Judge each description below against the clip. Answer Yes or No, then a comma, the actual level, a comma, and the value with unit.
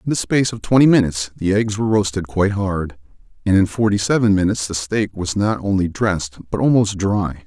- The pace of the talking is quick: Yes, fast, 210 wpm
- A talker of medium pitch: No, low, 100 Hz